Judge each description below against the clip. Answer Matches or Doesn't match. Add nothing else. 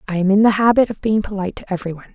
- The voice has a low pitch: Doesn't match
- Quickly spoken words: Matches